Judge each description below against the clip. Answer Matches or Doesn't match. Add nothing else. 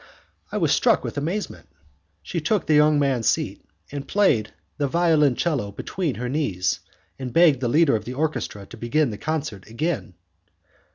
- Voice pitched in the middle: Matches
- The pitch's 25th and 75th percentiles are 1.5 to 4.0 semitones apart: Doesn't match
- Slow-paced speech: Doesn't match